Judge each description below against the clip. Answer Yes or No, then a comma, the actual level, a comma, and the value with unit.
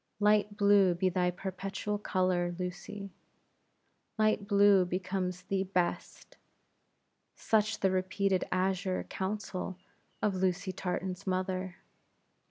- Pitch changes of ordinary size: No, narrow, 1.6 semitones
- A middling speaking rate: No, slow, 100 wpm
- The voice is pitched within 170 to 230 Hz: Yes, high, 190 Hz